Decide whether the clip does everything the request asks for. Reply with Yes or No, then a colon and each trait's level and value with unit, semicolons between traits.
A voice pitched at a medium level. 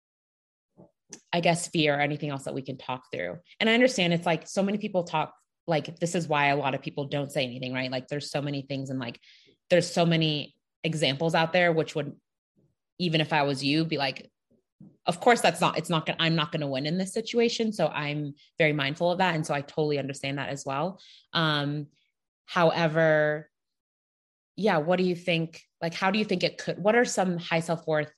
Yes: medium, 160 Hz